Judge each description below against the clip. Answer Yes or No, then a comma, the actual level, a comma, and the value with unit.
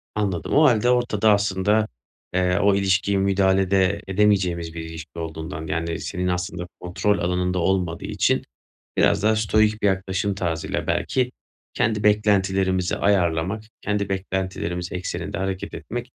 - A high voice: No, very low, 95 Hz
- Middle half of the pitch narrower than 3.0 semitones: Yes, narrow, 2.4 semitones